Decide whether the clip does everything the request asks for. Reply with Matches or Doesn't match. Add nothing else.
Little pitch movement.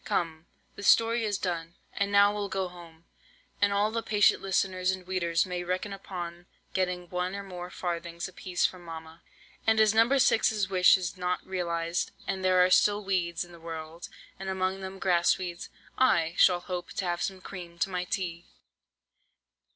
Matches